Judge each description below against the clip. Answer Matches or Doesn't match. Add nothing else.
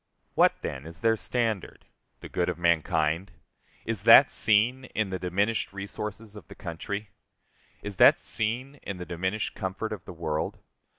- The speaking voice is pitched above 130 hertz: Doesn't match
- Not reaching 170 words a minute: Matches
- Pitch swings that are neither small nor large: Matches